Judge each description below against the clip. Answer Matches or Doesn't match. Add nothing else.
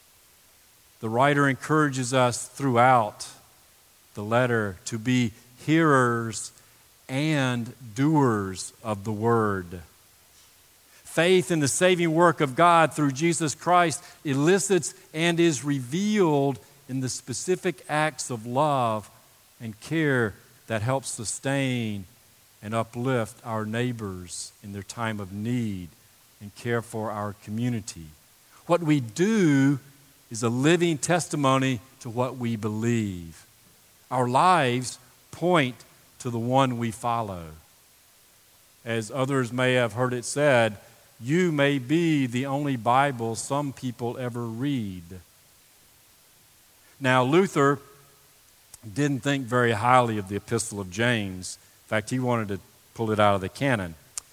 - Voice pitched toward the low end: Matches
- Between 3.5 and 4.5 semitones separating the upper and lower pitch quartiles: Matches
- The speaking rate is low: Matches